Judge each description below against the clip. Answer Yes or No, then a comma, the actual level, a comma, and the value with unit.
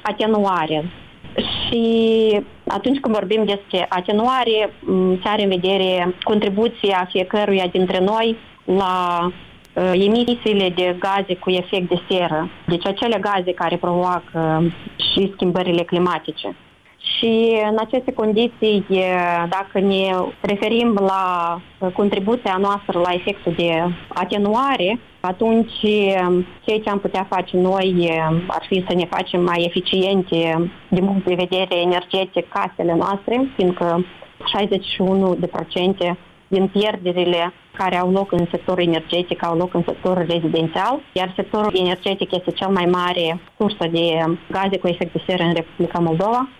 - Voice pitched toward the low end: No, medium, 185 Hz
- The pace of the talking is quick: No, average, 125 wpm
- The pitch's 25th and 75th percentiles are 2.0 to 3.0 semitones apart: Yes, average, 2.7 semitones